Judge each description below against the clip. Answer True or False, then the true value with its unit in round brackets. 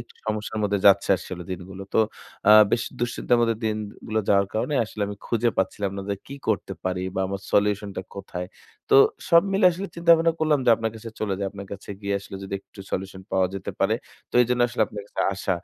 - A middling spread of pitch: True (3.2 semitones)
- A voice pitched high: False (105 Hz)